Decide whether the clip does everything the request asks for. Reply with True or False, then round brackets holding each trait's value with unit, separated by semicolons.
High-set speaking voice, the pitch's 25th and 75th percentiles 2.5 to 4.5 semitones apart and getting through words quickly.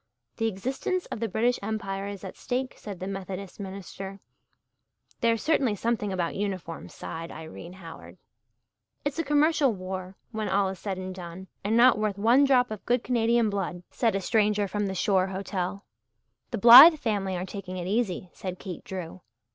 False (200 Hz; 3.6 semitones; 175 wpm)